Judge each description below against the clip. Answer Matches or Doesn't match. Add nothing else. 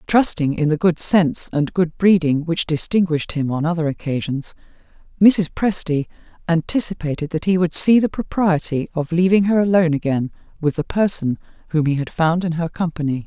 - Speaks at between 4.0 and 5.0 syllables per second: Doesn't match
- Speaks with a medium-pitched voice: Matches